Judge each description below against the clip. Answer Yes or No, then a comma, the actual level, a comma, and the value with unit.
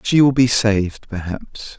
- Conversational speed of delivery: Yes, average, 170 wpm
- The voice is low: Yes, low, 110 Hz